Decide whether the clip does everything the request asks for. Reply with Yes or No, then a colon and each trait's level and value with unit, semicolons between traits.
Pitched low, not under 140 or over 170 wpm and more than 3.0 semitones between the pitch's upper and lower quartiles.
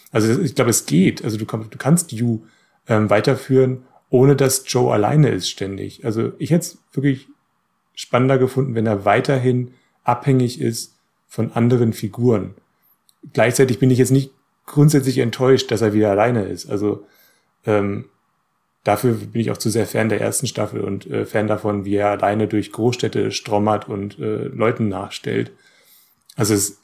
Yes: low, 115 Hz; average, 165 wpm; average, 3.9 semitones